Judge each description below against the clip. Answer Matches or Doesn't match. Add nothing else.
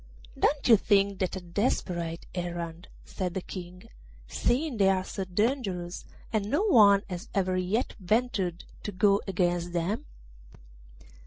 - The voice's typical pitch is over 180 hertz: Matches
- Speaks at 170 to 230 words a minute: Doesn't match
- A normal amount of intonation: Matches